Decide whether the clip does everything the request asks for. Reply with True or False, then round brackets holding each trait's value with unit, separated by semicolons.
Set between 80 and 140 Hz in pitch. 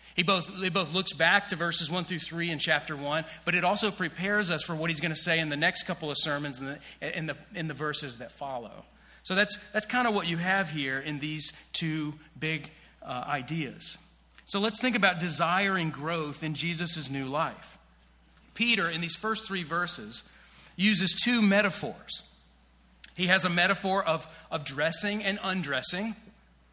False (170 Hz)